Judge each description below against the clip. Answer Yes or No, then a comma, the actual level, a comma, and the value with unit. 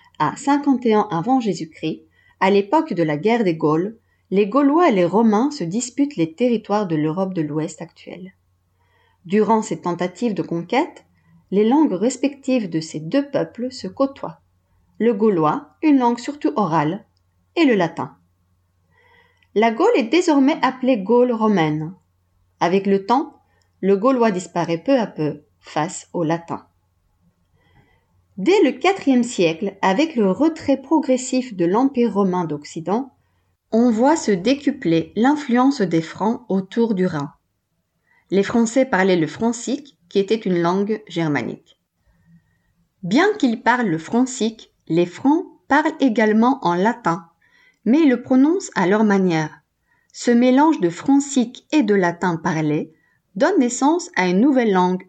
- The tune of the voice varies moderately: No, wide, 7.7 semitones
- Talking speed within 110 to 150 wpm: Yes, slow, 145 wpm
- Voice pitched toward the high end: Yes, high, 205 Hz